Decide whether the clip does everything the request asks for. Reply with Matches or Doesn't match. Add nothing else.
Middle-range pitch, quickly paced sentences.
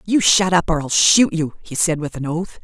Matches